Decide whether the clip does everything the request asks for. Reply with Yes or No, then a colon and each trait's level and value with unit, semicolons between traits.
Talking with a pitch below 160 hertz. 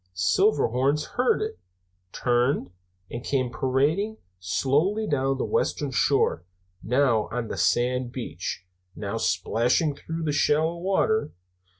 Yes: low, 135 Hz